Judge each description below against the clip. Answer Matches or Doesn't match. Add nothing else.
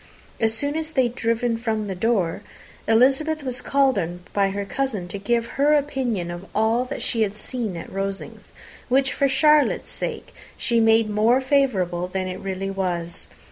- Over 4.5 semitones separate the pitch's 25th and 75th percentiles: Matches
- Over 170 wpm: Matches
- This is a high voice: Matches